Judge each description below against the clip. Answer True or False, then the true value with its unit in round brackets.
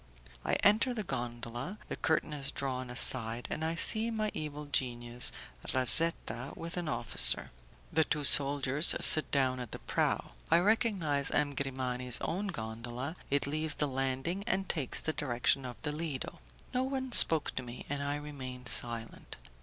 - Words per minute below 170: True (160 wpm)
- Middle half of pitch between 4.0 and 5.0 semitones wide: True (4.5 semitones)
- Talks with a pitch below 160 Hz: True (140 Hz)